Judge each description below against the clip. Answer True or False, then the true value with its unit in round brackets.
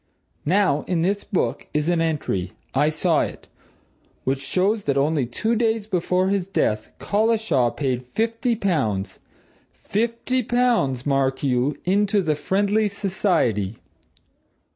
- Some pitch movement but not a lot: False (7.1 semitones)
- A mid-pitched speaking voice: True (180 Hz)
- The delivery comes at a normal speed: False (125 wpm)